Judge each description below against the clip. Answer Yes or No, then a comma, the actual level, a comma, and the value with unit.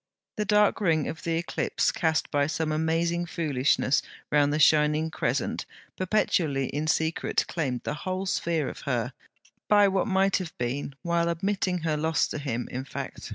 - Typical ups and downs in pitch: Yes, average, 3.3 semitones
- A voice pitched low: No, medium, 160 Hz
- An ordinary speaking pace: Yes, average, 165 wpm